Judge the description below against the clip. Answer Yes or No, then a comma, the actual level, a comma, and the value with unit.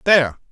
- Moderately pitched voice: Yes, medium, 150 Hz